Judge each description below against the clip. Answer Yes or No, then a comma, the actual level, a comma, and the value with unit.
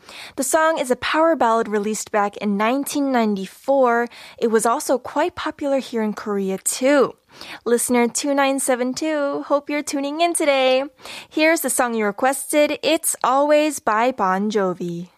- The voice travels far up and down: No, average, 4.7 semitones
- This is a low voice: No, very high, 260 Hz